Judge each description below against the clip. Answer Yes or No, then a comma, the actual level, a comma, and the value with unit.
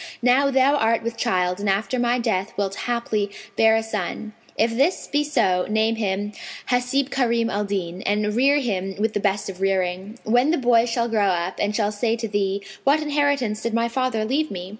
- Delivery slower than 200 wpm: No, fast, 205 wpm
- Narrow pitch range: No, average, 3.6 semitones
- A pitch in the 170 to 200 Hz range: No, high, 225 Hz